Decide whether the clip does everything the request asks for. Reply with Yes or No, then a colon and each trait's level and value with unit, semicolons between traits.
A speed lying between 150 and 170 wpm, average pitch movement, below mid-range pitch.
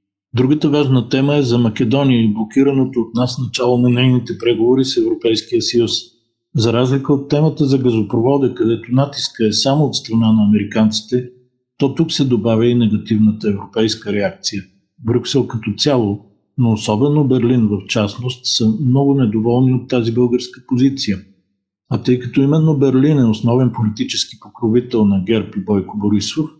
Yes: average, 155 wpm; average, 3.6 semitones; low, 125 Hz